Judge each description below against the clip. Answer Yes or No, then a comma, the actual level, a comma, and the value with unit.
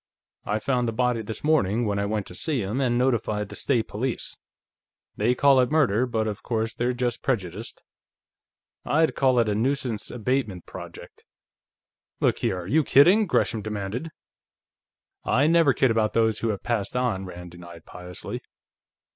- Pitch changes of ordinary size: Yes, average, 3.8 semitones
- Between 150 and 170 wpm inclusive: Yes, average, 165 wpm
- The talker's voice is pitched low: Yes, low, 115 Hz